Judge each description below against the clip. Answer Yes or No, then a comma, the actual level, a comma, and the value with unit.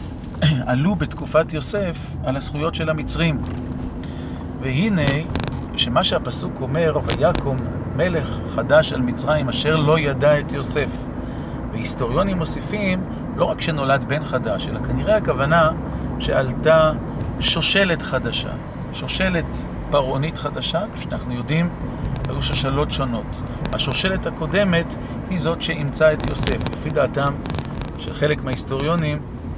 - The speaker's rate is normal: Yes, average, 110 wpm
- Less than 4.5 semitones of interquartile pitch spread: Yes, average, 4.0 semitones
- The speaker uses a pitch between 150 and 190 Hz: No, medium, 140 Hz